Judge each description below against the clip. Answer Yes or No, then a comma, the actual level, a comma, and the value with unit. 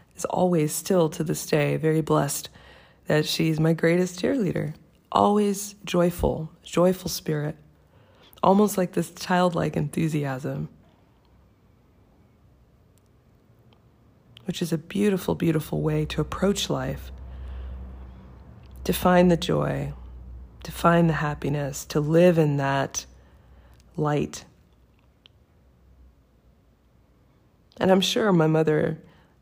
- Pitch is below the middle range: No, medium, 155 Hz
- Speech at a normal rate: No, slow, 100 wpm